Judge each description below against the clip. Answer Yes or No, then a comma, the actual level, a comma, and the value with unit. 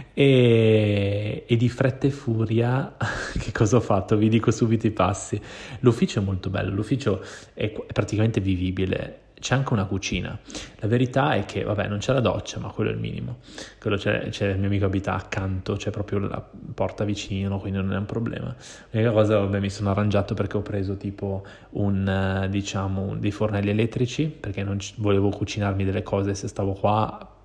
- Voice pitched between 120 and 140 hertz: No, low, 105 Hz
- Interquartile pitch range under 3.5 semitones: Yes, narrow, 2.5 semitones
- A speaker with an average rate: No, fast, 190 wpm